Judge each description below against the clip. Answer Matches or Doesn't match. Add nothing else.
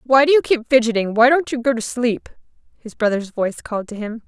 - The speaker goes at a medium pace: Doesn't match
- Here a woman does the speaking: Matches